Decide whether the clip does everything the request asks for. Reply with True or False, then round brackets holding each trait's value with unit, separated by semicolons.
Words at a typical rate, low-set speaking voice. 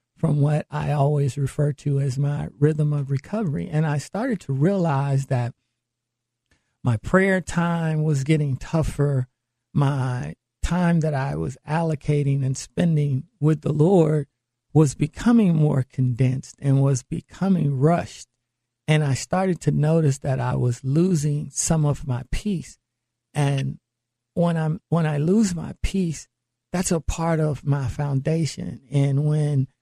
False (145 wpm; 145 Hz)